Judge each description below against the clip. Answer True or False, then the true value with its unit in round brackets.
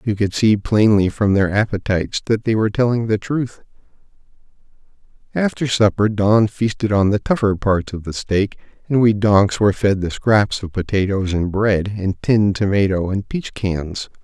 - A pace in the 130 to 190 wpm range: True (175 wpm)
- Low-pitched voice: True (105 Hz)